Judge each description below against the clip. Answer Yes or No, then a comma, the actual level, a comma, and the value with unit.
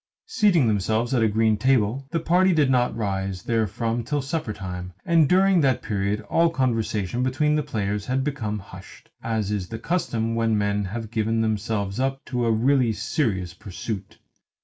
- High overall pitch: No, low, 115 Hz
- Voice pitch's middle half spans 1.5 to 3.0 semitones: No, average, 4.5 semitones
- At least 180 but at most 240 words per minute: No, average, 170 wpm